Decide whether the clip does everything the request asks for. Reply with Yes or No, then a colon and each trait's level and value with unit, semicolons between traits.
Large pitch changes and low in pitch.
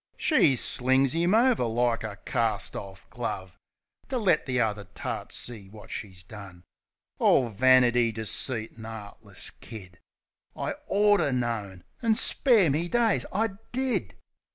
Yes: wide, 8.6 semitones; low, 120 Hz